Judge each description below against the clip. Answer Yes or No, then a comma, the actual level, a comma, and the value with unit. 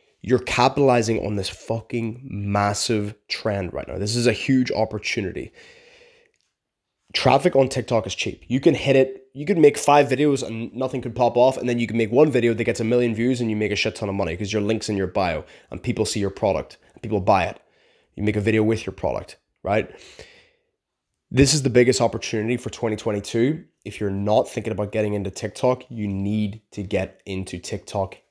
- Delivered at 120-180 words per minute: No, fast, 205 wpm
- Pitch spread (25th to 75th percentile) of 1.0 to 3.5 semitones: No, average, 3.9 semitones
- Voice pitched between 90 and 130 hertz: Yes, low, 115 Hz